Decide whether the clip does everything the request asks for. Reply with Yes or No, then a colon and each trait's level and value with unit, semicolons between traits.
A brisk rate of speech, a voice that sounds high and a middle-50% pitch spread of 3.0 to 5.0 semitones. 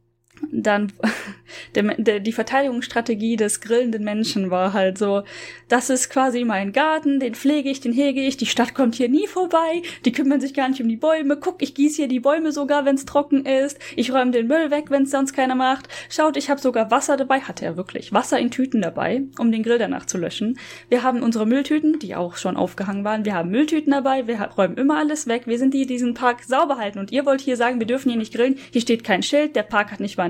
Yes: fast, 240 wpm; very high, 255 Hz; average, 3.8 semitones